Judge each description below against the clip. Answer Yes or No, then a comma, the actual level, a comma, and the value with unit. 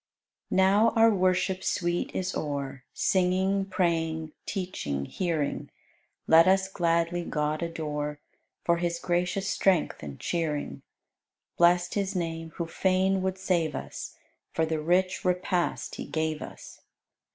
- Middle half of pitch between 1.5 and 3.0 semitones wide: Yes, average, 2.7 semitones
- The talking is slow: Yes, slow, 130 wpm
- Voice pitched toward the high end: No, medium, 175 Hz